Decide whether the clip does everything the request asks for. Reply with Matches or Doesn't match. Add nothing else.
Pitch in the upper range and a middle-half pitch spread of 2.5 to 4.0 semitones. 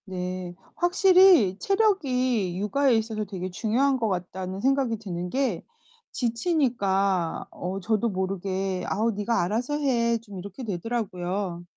Doesn't match